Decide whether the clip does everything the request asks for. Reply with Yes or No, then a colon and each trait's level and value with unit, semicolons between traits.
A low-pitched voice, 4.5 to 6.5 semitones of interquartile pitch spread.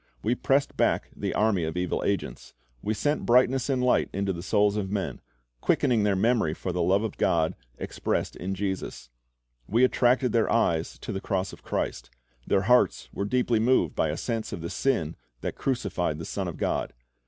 Yes: low, 100 Hz; average, 5.1 semitones